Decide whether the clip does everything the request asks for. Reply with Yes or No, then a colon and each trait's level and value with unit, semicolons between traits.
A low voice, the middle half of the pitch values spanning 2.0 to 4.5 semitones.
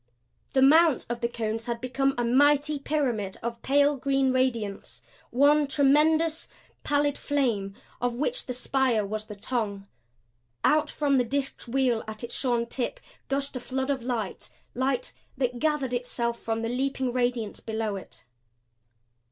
No: very high, 255 Hz; average, 3.1 semitones